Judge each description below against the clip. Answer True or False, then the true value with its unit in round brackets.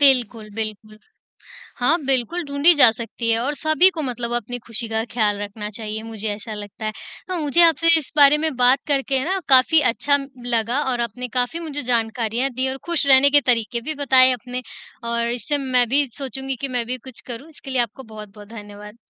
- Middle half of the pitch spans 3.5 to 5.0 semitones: True (3.8 semitones)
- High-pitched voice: True (250 Hz)